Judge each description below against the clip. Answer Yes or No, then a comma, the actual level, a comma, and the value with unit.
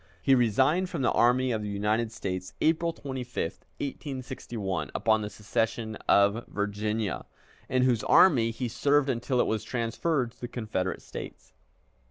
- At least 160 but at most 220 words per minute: No, average, 150 wpm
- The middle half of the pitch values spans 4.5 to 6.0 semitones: No, average, 3.8 semitones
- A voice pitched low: Yes, low, 115 Hz